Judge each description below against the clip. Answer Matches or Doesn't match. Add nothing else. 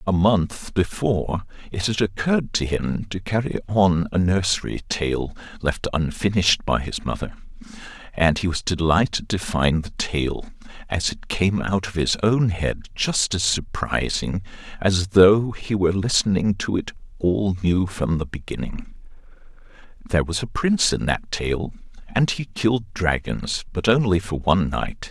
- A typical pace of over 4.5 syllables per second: Doesn't match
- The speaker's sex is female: Doesn't match